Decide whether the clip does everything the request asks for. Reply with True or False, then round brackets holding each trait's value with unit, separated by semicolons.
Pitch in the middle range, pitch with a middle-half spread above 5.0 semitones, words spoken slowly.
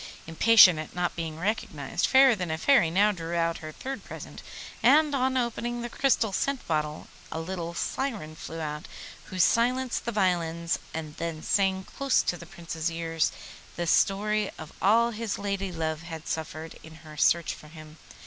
False (175 Hz; 5.6 semitones; 175 wpm)